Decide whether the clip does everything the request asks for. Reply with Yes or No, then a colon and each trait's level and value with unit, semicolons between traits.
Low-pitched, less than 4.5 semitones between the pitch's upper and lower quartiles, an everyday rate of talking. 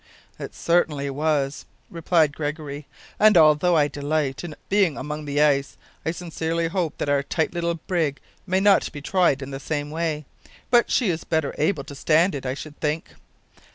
No: medium, 155 Hz; average, 2.8 semitones; average, 180 wpm